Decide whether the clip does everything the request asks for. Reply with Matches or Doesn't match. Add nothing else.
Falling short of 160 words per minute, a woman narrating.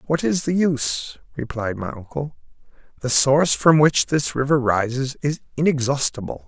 Doesn't match